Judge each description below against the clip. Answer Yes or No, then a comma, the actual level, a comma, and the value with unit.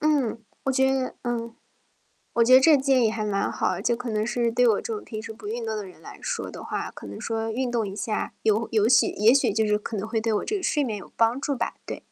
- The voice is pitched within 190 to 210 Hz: No, high, 230 Hz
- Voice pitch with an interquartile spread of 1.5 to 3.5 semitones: Yes, average, 2.9 semitones